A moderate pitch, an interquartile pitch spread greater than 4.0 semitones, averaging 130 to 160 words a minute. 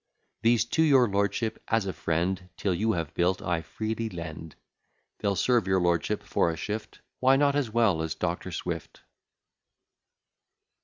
No: low, 100 Hz; average, 4.8 semitones; average, 155 wpm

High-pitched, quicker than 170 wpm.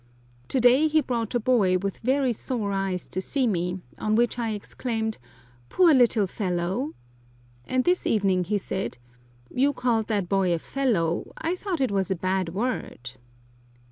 No: high, 220 Hz; average, 165 wpm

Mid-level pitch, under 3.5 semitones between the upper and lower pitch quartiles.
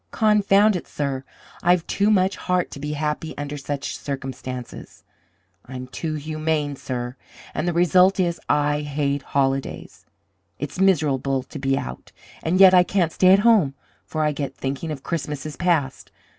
No: medium, 150 Hz; average, 4.4 semitones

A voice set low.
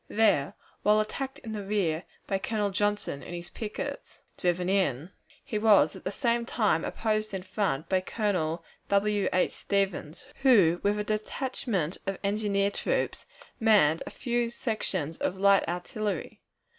No: high, 200 Hz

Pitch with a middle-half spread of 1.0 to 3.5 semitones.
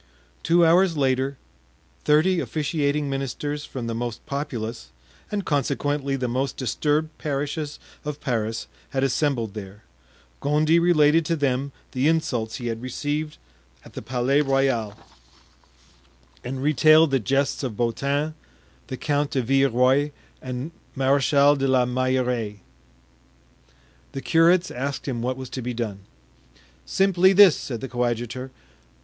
Yes: average, 3.2 semitones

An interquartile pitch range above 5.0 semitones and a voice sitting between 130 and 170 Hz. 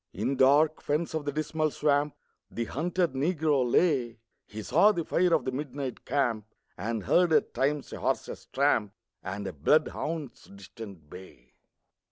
Yes: wide, 5.4 semitones; medium, 140 Hz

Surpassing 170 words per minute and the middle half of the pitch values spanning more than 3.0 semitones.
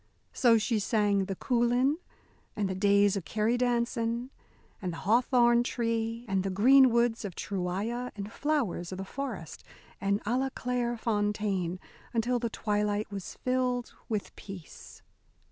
No: average, 150 wpm; average, 3.4 semitones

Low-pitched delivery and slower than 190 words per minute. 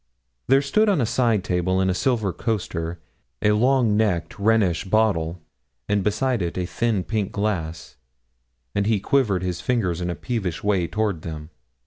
Yes: low, 100 Hz; average, 165 wpm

